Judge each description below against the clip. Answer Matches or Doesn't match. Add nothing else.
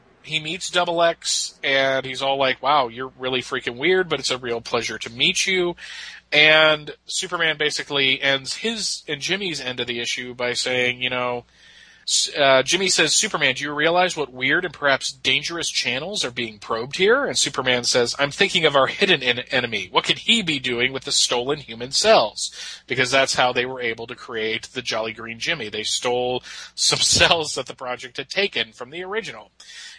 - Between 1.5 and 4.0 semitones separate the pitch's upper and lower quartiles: Doesn't match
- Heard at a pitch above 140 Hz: Doesn't match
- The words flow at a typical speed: Matches